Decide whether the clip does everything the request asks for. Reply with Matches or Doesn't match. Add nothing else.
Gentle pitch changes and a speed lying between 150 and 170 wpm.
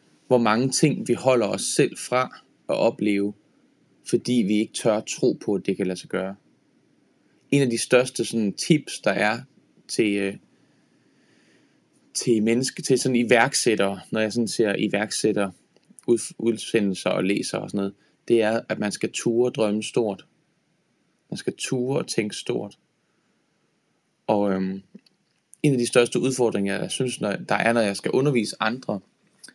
Doesn't match